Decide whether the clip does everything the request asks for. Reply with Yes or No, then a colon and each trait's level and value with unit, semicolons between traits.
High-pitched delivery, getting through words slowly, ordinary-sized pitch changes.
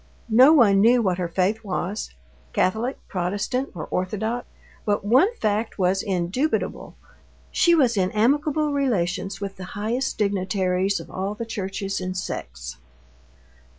Yes: high, 200 Hz; slow, 125 wpm; average, 4.3 semitones